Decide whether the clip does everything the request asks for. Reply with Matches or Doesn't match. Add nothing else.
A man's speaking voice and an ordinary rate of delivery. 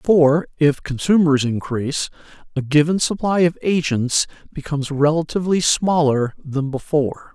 Doesn't match